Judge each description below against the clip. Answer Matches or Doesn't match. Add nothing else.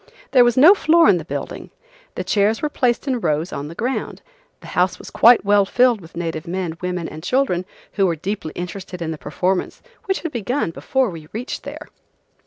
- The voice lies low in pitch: Doesn't match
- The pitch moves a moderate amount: Doesn't match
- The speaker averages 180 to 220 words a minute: Matches